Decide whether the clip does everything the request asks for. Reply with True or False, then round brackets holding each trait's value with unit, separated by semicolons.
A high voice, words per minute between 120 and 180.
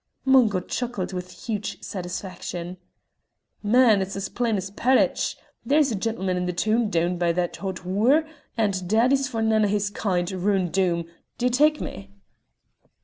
True (200 Hz; 155 wpm)